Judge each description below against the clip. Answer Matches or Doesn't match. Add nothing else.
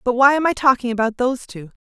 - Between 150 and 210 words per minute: Doesn't match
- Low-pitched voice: Doesn't match